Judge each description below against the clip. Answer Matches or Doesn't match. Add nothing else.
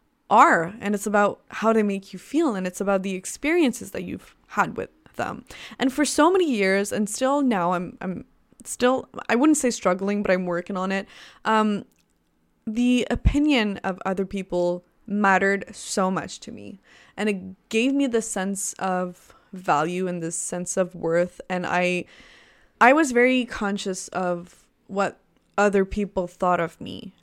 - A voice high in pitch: Matches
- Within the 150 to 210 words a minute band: Matches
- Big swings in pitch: Doesn't match